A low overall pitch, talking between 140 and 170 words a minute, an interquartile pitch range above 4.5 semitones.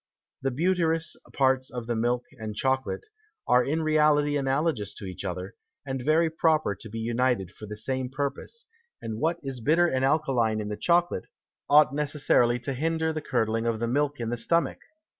No: low, 130 Hz; average, 180 wpm; average, 5.0 semitones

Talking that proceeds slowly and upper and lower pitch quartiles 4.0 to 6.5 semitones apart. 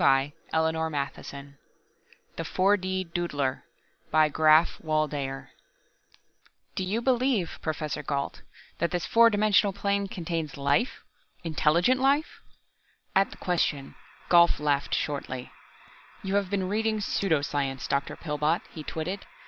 Yes: slow, 130 wpm; average, 5.2 semitones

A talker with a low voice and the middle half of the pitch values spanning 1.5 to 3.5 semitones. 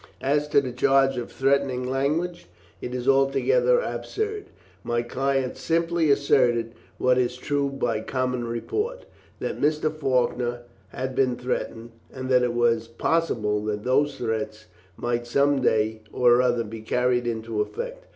Yes: low, 125 Hz; average, 2.9 semitones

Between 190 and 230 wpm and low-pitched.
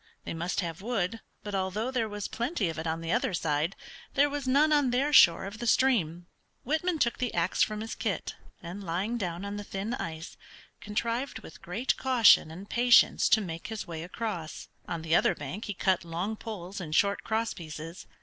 No: average, 200 wpm; high, 200 Hz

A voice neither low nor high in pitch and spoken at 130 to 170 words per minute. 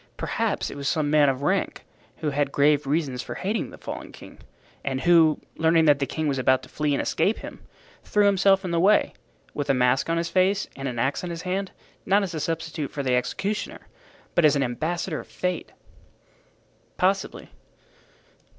No: medium, 155 Hz; average, 190 wpm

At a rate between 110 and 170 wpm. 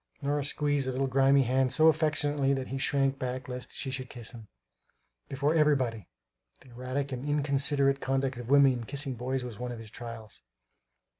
No: average, 180 wpm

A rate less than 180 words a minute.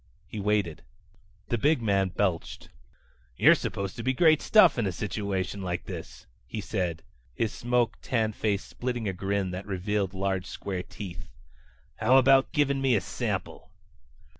Yes: average, 160 wpm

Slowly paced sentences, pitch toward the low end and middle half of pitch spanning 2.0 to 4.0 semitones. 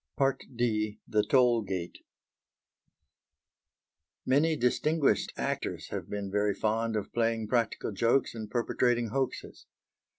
Yes: slow, 105 wpm; low, 115 Hz; average, 2.7 semitones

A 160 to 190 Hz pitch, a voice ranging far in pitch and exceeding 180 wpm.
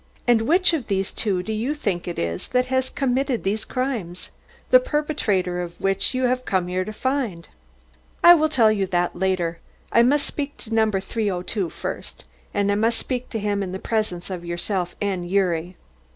No: high, 205 Hz; wide, 5.7 semitones; average, 190 wpm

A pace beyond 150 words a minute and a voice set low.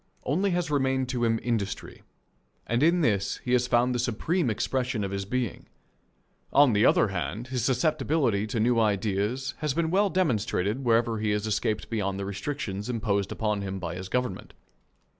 Yes: average, 175 wpm; low, 115 Hz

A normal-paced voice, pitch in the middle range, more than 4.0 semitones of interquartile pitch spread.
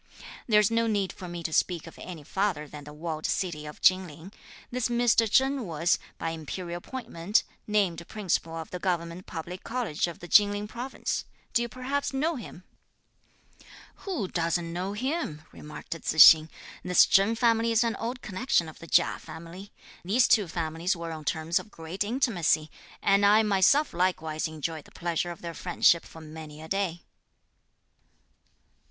Yes: average, 170 wpm; medium, 180 Hz; average, 4.8 semitones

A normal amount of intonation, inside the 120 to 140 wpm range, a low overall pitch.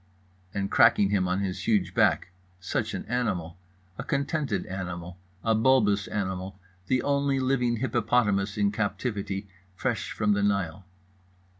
Yes: average, 4.3 semitones; slow, 135 wpm; low, 100 Hz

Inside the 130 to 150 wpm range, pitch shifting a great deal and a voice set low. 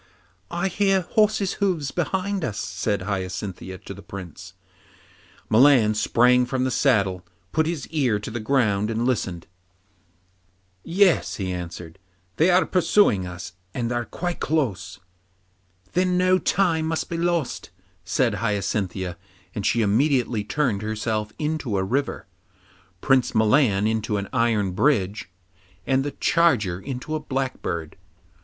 Yes: slow, 135 wpm; wide, 7.8 semitones; low, 120 Hz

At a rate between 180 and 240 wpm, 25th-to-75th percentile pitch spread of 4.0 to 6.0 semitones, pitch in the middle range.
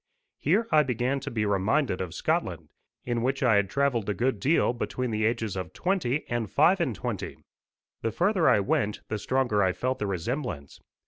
No: average, 190 wpm; average, 5.1 semitones; low, 120 Hz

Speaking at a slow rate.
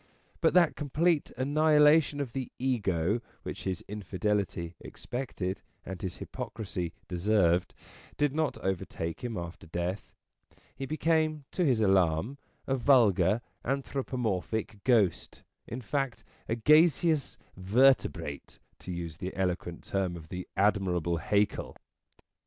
Yes: slow, 120 wpm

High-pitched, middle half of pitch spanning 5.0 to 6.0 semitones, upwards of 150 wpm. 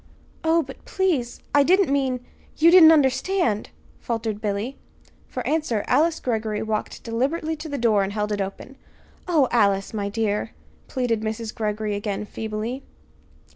No: high, 230 Hz; wide, 5.4 semitones; average, 145 wpm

